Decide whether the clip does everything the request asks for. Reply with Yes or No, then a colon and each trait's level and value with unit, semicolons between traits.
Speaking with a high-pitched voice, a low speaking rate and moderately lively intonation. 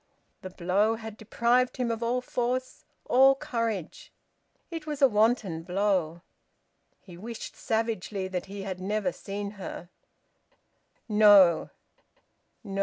Yes: high, 210 Hz; slow, 120 wpm; average, 3.8 semitones